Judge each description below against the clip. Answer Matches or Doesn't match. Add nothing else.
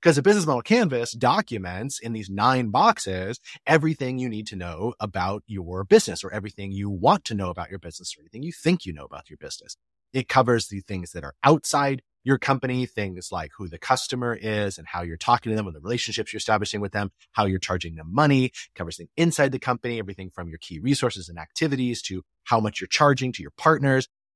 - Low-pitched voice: Matches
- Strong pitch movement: Matches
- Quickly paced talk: Matches